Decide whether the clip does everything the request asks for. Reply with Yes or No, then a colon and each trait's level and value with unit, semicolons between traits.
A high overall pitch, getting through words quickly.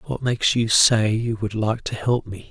No: low, 110 Hz; fast, 240 wpm